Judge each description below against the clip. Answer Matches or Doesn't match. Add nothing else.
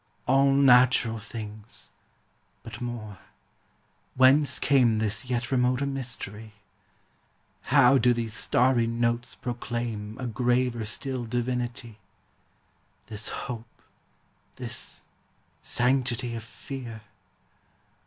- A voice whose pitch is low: Matches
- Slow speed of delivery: Matches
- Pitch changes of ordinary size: Doesn't match